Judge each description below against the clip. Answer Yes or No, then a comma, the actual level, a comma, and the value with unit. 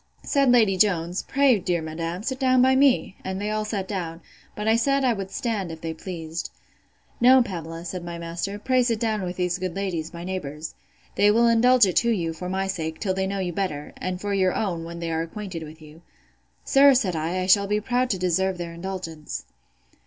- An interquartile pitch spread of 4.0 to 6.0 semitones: Yes, average, 4.3 semitones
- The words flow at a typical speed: No, fast, 215 wpm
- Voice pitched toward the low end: No, high, 190 Hz